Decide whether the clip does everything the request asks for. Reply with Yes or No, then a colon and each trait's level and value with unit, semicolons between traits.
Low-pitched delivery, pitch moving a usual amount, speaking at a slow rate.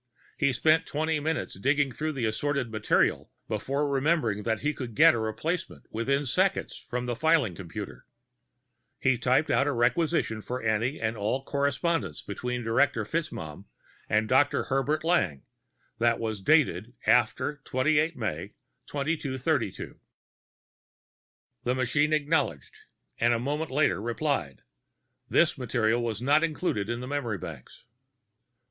Yes: low, 130 Hz; average, 4.8 semitones; slow, 130 wpm